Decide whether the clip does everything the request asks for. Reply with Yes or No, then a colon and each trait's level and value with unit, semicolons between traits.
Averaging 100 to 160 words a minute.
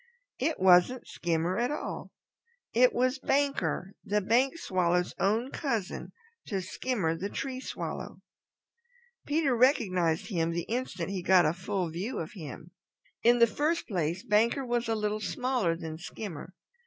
Yes: average, 145 wpm